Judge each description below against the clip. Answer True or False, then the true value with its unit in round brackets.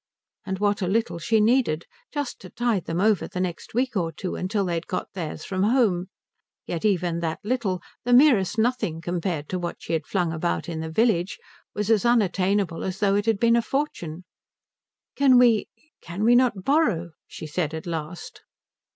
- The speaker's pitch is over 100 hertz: True (190 Hz)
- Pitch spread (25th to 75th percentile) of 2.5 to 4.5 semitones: False (5.1 semitones)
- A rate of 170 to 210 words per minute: True (190 wpm)